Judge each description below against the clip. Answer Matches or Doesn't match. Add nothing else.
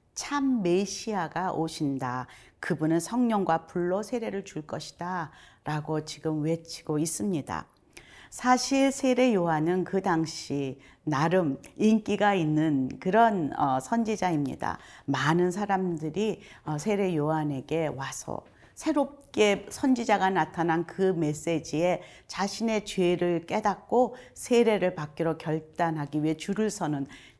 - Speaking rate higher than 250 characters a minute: Doesn't match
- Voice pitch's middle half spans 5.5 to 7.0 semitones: Doesn't match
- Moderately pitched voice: Matches